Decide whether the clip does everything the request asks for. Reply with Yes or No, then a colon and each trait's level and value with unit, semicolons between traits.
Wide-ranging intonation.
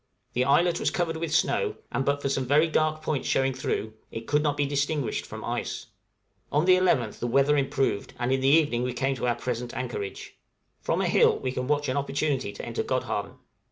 No: average, 3.0 semitones